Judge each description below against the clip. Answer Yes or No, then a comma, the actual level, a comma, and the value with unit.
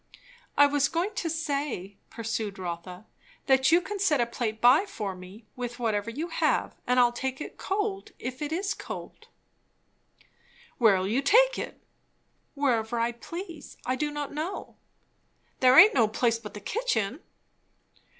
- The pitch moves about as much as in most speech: No, wide, 6.4 semitones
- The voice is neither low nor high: No, very high, 255 Hz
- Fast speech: No, average, 155 wpm